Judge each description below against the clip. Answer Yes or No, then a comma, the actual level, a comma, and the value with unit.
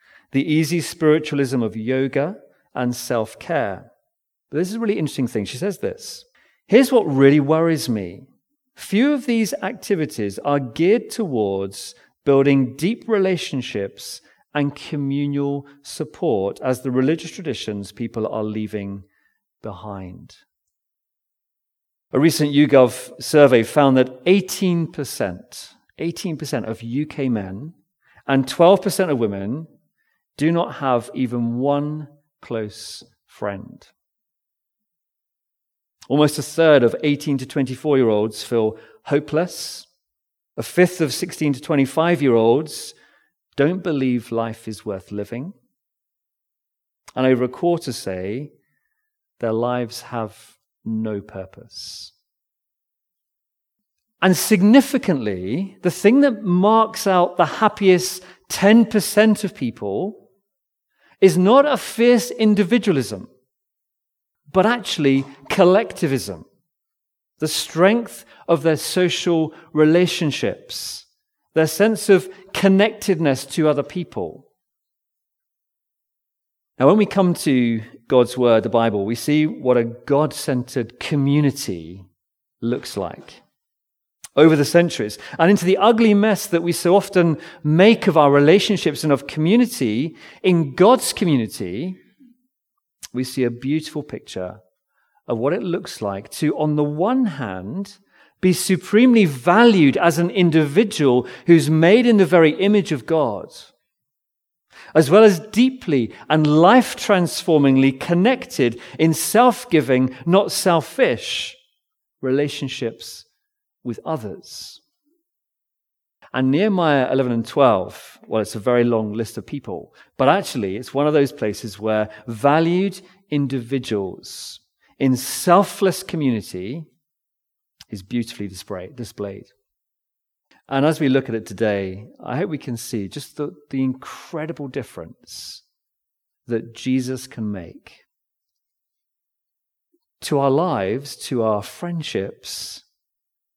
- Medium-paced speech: No, slow, 115 wpm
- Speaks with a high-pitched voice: No, medium, 150 Hz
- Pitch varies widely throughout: Yes, wide, 7.1 semitones